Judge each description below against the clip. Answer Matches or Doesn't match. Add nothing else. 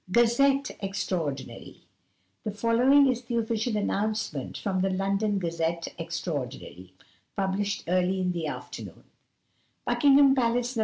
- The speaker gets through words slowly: Matches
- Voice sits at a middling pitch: Doesn't match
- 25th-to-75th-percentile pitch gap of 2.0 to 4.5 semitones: Doesn't match